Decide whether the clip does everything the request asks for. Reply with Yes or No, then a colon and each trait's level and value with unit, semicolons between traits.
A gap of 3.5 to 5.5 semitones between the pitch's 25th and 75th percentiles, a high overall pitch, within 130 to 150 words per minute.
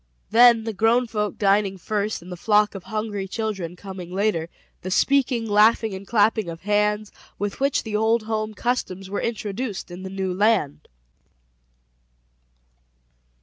No: narrow, 2.6 semitones; high, 210 Hz; average, 145 wpm